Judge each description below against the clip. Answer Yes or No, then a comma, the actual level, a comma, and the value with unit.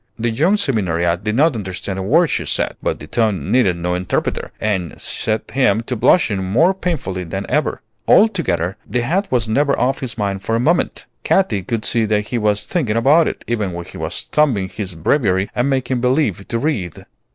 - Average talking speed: Yes, average, 195 wpm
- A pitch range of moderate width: No, wide, 6.0 semitones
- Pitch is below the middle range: Yes, low, 110 Hz